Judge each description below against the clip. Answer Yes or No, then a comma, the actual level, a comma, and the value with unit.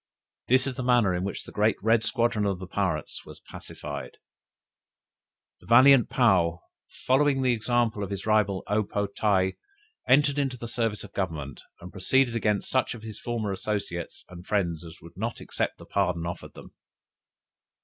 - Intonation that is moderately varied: Yes, average, 4.3 semitones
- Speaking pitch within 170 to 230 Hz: No, low, 105 Hz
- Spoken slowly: No, average, 170 wpm